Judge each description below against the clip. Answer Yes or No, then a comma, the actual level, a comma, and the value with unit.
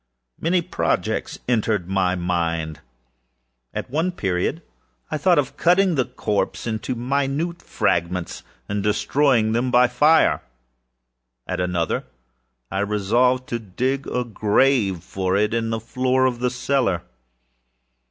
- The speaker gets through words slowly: Yes, slow, 125 wpm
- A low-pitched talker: Yes, low, 120 Hz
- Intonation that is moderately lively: No, wide, 5.7 semitones